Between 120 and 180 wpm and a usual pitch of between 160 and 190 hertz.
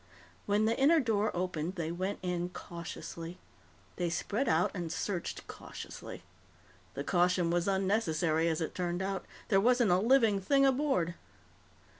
Yes: average, 145 wpm; medium, 185 Hz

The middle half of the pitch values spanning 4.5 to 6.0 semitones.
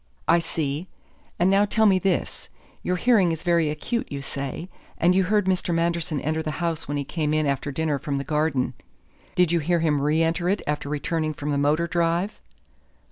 No: average, 3.0 semitones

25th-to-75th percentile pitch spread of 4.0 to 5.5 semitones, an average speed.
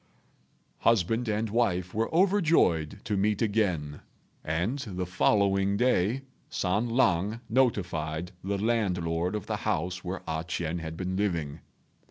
No: average, 4.5 semitones; slow, 130 wpm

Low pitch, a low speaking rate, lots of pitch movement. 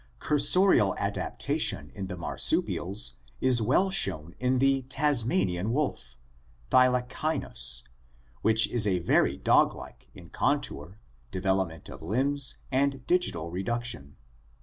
Yes: low, 115 Hz; slow, 105 wpm; wide, 7.5 semitones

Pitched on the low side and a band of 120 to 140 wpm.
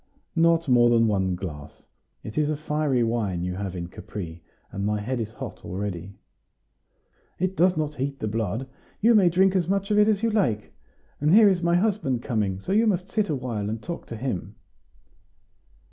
No: low, 130 Hz; average, 195 wpm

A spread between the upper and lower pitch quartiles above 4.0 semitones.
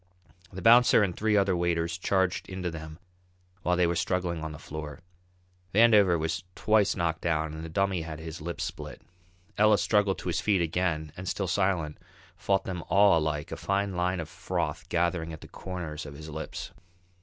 No: average, 3.3 semitones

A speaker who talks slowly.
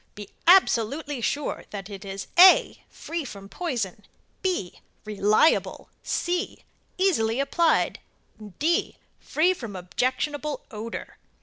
Yes: slow, 105 wpm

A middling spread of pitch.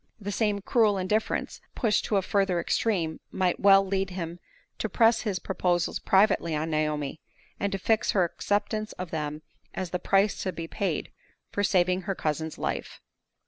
Yes: average, 3.2 semitones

